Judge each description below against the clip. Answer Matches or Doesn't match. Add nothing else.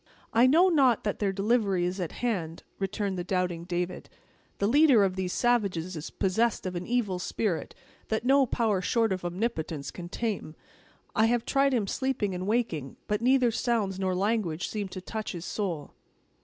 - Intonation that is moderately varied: Matches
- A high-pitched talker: Matches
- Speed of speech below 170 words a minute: Doesn't match